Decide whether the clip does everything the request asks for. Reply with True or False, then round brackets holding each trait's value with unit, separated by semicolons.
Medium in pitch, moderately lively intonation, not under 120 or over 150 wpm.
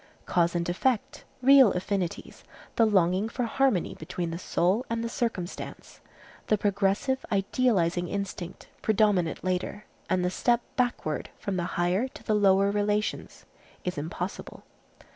False (195 Hz; 3.9 semitones; 135 wpm)